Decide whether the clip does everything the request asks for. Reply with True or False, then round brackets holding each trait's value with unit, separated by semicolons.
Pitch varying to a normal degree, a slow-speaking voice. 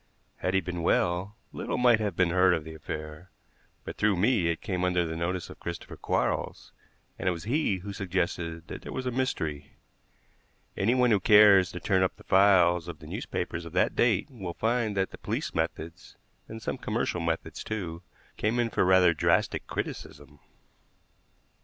False (3.9 semitones; 185 wpm)